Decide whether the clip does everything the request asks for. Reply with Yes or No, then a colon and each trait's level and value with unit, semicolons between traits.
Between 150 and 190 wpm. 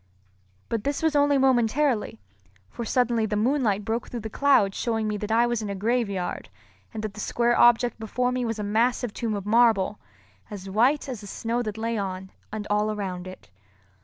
No: average, 200 wpm